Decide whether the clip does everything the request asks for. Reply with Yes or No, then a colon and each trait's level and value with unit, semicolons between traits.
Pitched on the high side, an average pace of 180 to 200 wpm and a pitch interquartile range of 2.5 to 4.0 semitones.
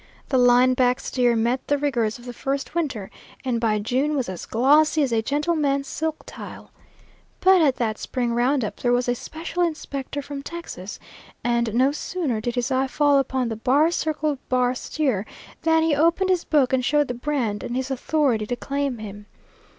Yes: very high, 260 Hz; average, 190 wpm; average, 3.6 semitones